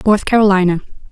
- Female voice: Yes, female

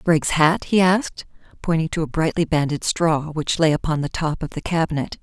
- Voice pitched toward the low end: No, medium, 160 Hz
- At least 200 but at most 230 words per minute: Yes, fast, 205 wpm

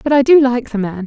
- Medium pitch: No, high, 245 Hz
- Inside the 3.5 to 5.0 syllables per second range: No, 5.8 syllables/s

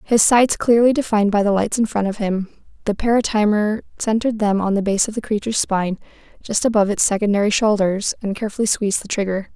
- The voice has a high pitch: Yes, high, 210 Hz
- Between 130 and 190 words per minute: No, average, 200 wpm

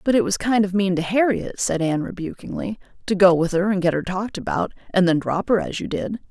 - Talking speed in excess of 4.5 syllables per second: Yes, 6.0 syllables/s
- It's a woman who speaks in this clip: Yes, female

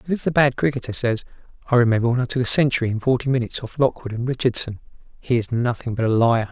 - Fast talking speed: Yes, fast, 240 wpm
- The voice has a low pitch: Yes, low, 125 Hz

